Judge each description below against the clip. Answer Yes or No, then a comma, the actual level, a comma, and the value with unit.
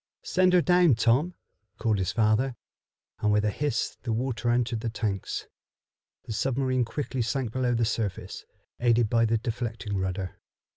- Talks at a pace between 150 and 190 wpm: Yes, average, 155 wpm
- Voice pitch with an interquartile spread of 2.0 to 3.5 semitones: Yes, average, 3.1 semitones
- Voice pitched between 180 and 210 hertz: No, low, 115 Hz